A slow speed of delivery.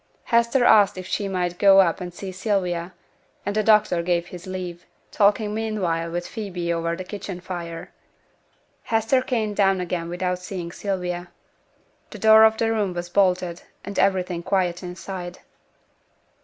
No: average, 155 wpm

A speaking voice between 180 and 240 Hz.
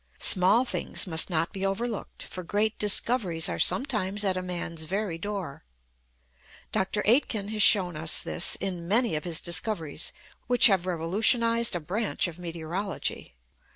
Yes: high, 190 Hz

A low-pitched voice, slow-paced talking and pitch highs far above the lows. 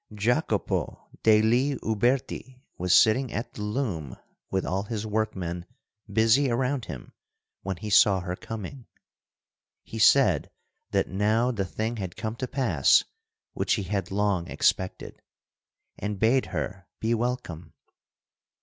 No: low, 110 Hz; slow, 130 wpm; average, 3.9 semitones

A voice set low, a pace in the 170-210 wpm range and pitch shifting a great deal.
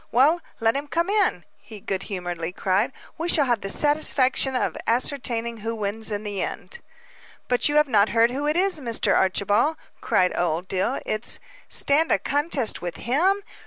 No: high, 235 Hz; average, 180 wpm; wide, 6.4 semitones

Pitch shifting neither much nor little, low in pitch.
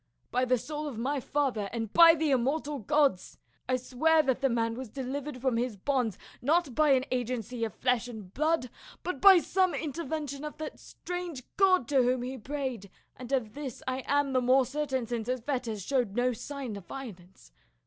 No: average, 3.5 semitones; very high, 260 Hz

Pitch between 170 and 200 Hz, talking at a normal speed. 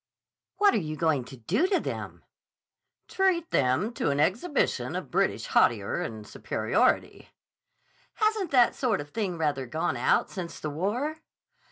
Yes: high, 190 Hz; average, 150 wpm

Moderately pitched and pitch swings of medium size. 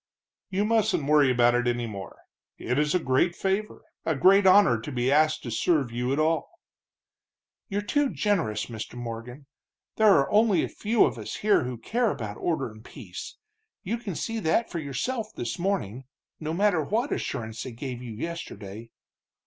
No: medium, 150 Hz; wide, 8.7 semitones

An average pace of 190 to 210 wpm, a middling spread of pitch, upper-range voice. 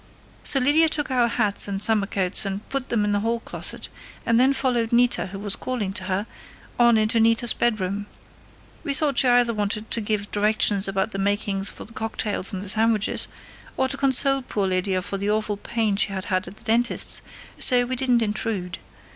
Yes: average, 200 wpm; average, 3.2 semitones; high, 215 Hz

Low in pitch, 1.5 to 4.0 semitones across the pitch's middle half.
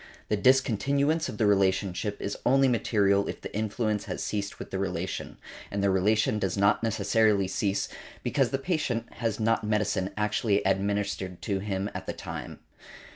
Yes: low, 105 Hz; narrow, 2.5 semitones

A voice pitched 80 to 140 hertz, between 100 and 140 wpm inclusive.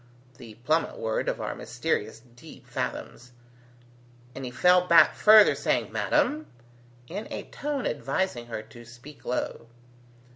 Yes: low, 135 Hz; slow, 135 wpm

